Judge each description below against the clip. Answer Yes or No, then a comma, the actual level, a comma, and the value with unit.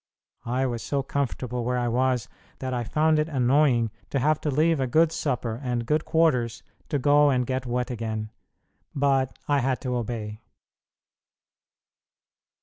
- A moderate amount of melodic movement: Yes, average, 3.1 semitones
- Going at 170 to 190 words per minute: No, average, 155 wpm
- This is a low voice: Yes, low, 130 Hz